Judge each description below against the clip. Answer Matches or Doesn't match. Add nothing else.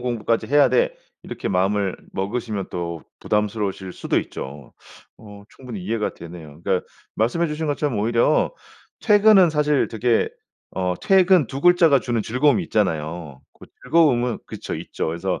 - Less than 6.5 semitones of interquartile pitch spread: Doesn't match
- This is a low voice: Matches